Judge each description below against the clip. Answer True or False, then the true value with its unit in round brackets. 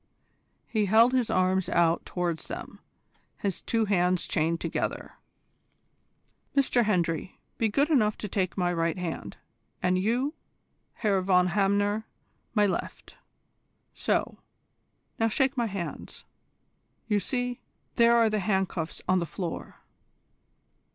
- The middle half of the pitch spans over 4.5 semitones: False (3.9 semitones)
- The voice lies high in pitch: True (195 Hz)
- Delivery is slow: True (125 wpm)